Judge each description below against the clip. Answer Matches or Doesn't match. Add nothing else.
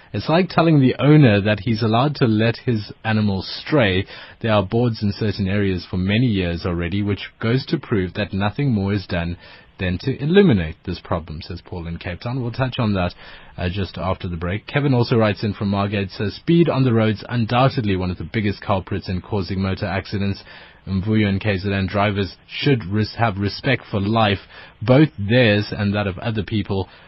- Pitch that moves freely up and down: Doesn't match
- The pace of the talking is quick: Doesn't match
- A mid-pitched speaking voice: Doesn't match